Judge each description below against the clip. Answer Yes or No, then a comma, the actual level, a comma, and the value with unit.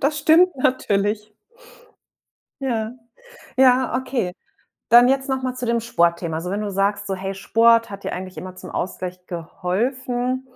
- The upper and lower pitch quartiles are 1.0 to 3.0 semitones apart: No, average, 5.2 semitones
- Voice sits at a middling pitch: No, high, 225 Hz